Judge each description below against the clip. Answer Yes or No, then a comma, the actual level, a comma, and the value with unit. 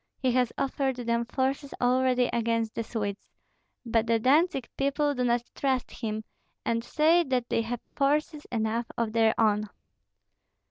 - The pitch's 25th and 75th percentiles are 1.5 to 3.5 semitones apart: Yes, average, 3.0 semitones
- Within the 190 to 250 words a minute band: No, average, 150 wpm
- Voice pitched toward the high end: Yes, high, 245 Hz